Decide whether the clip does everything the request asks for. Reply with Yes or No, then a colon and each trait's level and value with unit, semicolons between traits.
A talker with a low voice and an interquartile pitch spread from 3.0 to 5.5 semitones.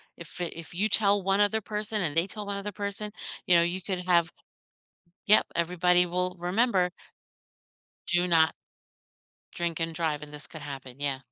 No: medium, 180 Hz; average, 3.3 semitones